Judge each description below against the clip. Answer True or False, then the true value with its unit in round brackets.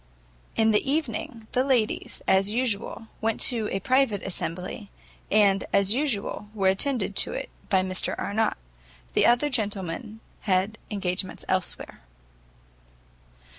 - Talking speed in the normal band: False (125 wpm)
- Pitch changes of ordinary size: True (3.5 semitones)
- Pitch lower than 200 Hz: False (210 Hz)